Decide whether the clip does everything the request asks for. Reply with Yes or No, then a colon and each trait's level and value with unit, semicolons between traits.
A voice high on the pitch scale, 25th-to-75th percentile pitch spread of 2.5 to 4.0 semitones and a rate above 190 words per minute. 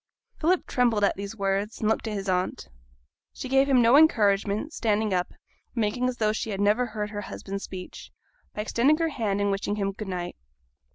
Yes: high, 210 Hz; average, 3.4 semitones; fast, 205 wpm